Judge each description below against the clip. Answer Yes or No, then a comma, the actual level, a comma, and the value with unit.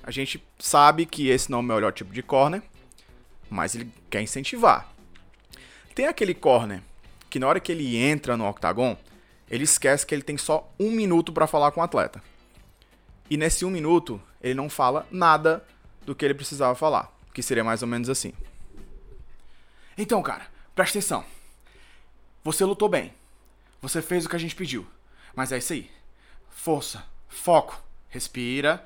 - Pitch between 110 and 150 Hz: Yes, medium, 140 Hz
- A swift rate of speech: No, average, 165 wpm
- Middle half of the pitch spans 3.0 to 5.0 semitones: No, wide, 5.4 semitones